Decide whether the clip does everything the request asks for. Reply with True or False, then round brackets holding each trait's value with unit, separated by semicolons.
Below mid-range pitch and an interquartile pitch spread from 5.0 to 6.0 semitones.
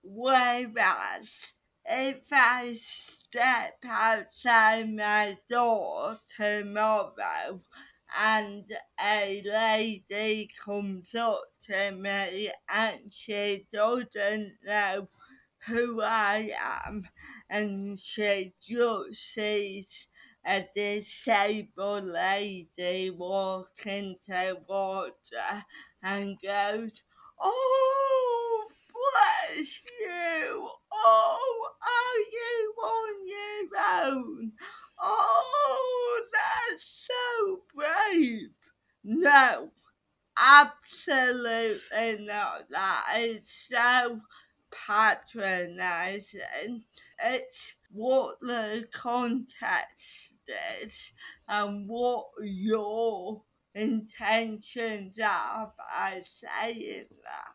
False (220 Hz; 5.6 semitones)